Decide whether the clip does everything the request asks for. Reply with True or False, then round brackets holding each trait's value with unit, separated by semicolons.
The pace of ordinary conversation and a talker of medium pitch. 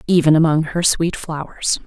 True (160 wpm; 160 Hz)